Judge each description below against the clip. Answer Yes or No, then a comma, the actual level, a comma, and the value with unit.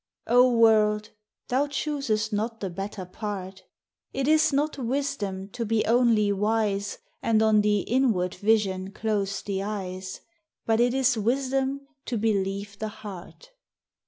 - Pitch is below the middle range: No, high, 215 Hz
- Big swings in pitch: No, average, 3.7 semitones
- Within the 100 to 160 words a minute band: Yes, slow, 135 wpm